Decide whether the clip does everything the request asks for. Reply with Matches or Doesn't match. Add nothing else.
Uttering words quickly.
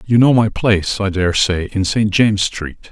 Matches